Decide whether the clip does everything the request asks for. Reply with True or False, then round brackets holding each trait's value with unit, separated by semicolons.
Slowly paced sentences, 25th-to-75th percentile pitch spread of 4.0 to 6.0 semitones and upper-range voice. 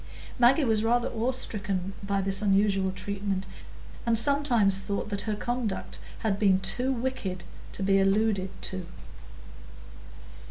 False (130 wpm; 3.2 semitones; 205 Hz)